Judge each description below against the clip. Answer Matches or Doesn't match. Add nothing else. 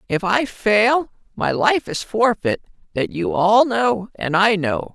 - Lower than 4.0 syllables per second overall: Matches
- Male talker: Matches